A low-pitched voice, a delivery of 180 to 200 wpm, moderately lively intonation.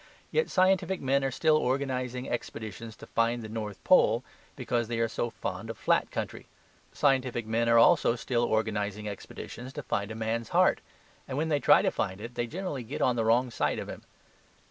Yes: low, 120 Hz; average, 195 wpm; average, 3.1 semitones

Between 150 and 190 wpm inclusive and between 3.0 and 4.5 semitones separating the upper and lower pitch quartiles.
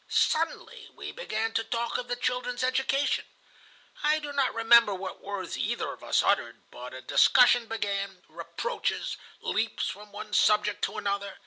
Yes: average, 155 wpm; average, 4.0 semitones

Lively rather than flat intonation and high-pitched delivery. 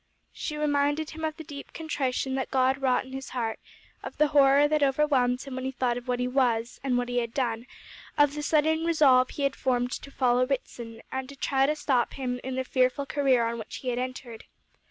No: narrow, 2.5 semitones; very high, 265 Hz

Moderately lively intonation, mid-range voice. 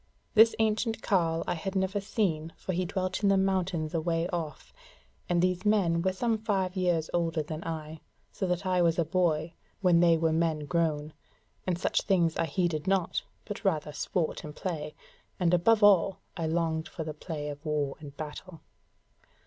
Yes: average, 3.0 semitones; medium, 170 Hz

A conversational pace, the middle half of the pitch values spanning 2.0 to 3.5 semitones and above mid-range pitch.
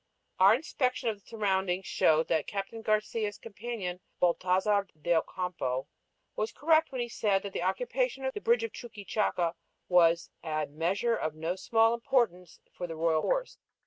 No: average, 160 wpm; average, 4.9 semitones; high, 200 Hz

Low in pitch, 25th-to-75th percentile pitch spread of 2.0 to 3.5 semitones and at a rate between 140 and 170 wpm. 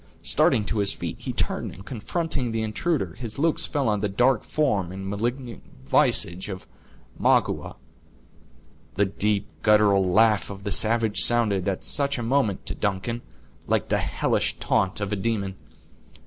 Yes: low, 105 Hz; average, 3.2 semitones; average, 160 wpm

